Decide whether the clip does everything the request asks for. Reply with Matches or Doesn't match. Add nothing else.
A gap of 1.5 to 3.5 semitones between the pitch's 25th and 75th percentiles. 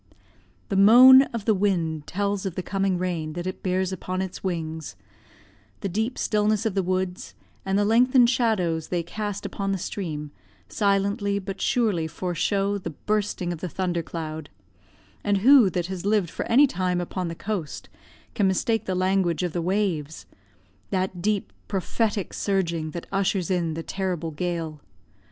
Matches